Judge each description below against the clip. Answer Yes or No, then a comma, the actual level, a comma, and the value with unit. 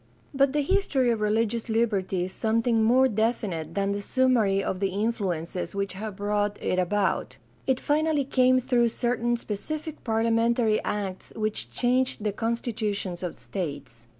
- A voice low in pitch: No, high, 220 Hz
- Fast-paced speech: No, average, 150 wpm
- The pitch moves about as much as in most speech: Yes, average, 3.6 semitones